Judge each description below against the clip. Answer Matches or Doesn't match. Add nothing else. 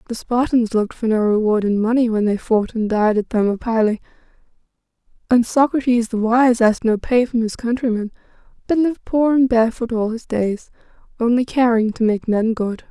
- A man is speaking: Doesn't match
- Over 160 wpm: Matches